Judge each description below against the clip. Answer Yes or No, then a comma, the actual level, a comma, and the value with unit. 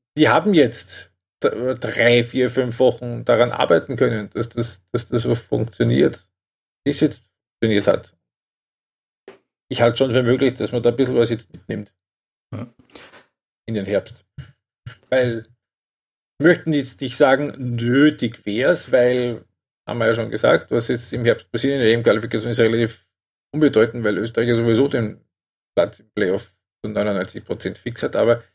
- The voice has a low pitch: Yes, low, 120 Hz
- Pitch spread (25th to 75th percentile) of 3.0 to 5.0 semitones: No, narrow, 2.4 semitones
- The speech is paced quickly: No, average, 160 wpm